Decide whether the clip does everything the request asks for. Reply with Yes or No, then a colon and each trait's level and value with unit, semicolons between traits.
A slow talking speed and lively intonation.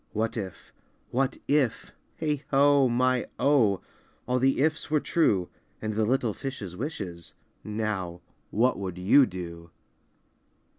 Yes: slow, 120 wpm; wide, 6.1 semitones